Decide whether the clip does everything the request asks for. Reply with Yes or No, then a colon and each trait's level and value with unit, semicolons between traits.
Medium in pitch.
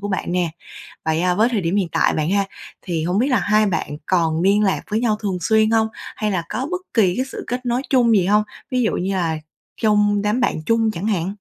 No: high, 205 Hz